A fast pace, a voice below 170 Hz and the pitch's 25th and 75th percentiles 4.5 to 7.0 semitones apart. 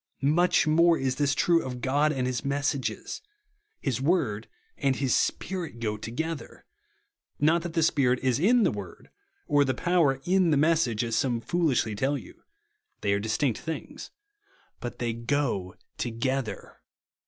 No: average, 155 wpm; low, 135 Hz; average, 5.2 semitones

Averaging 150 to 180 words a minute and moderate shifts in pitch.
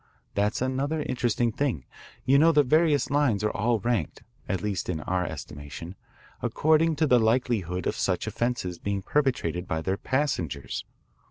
No: average, 155 wpm; wide, 7.4 semitones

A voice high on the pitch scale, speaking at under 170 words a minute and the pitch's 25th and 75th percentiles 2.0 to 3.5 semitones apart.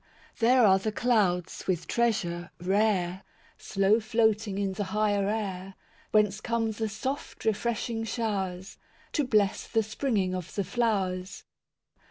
Yes: high, 210 Hz; slow, 135 wpm; average, 2.8 semitones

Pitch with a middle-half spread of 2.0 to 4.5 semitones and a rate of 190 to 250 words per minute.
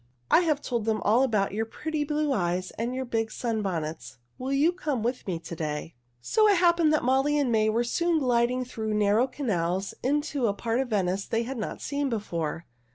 No: wide, 5.6 semitones; fast, 205 wpm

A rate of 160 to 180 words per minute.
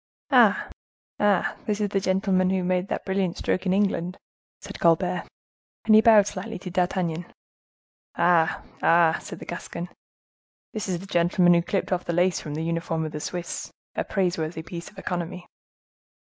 Yes: average, 170 wpm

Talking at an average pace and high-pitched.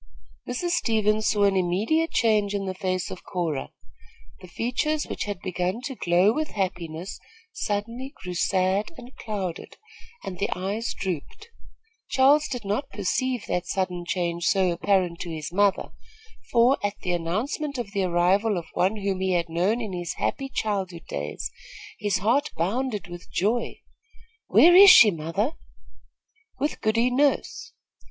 Yes: average, 150 wpm; high, 200 Hz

